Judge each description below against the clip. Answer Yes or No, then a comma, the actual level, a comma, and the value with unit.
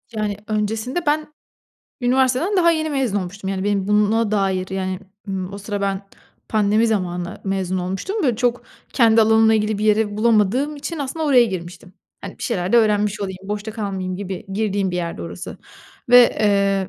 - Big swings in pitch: No, average, 3.5 semitones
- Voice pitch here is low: No, high, 210 Hz